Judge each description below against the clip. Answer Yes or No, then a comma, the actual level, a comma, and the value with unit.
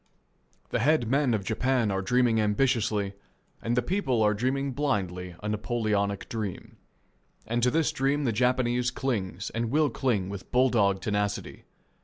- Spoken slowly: No, average, 155 wpm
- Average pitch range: Yes, average, 4.0 semitones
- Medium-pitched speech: No, low, 115 Hz